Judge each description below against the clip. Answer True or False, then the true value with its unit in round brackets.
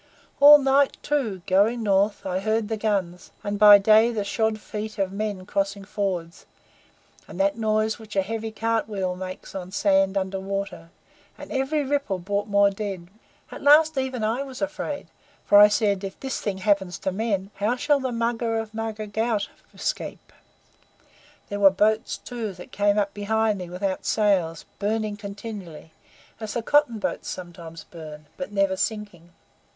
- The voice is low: False (205 Hz)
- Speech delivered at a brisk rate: False (165 wpm)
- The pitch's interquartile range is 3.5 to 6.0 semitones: False (2.6 semitones)